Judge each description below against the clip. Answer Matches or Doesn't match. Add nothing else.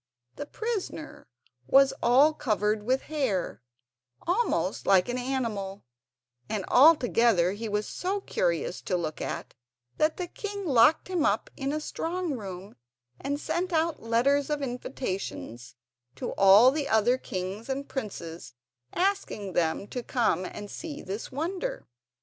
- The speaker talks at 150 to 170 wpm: Doesn't match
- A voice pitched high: Matches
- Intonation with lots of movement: Matches